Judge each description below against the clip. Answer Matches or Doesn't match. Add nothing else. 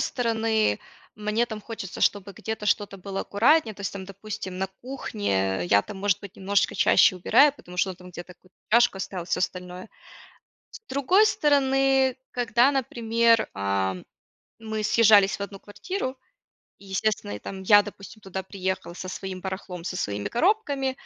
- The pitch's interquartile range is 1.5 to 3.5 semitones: Doesn't match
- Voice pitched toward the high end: Matches